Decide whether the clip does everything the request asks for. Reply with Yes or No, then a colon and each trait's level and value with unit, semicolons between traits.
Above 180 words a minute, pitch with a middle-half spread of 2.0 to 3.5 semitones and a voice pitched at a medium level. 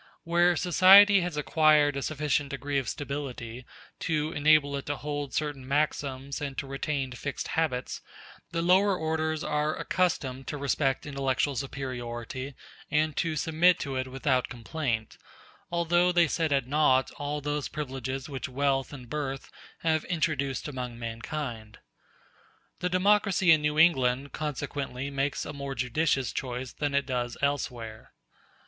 No: average, 140 wpm; average, 2.9 semitones; medium, 145 Hz